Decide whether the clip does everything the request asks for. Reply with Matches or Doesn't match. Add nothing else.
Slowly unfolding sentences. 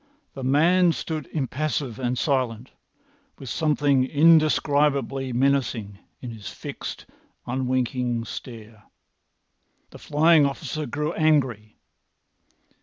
Matches